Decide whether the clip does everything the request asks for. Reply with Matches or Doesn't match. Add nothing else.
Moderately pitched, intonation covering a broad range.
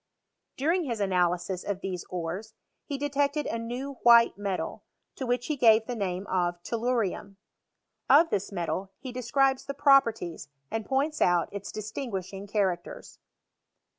Doesn't match